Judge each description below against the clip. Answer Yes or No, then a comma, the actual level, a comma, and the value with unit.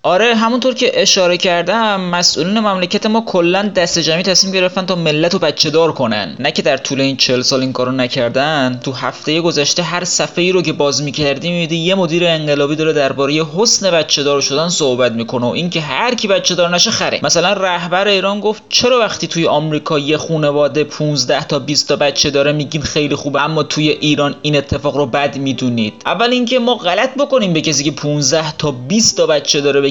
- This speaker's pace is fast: Yes, fast, 200 wpm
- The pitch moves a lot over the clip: No, average, 4.4 semitones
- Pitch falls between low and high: Yes, medium, 160 Hz